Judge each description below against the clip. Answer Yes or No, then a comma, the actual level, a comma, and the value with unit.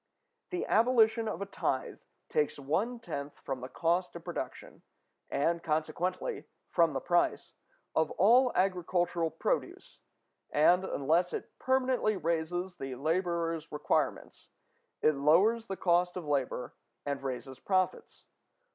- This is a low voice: No, medium, 175 Hz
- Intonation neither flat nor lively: Yes, average, 4.1 semitones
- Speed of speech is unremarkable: No, slow, 125 wpm